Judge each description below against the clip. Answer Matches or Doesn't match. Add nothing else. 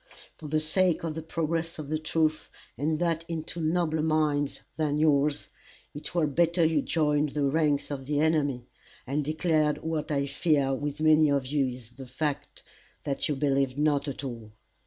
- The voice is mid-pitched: Matches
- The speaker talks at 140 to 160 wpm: Doesn't match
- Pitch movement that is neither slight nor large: Doesn't match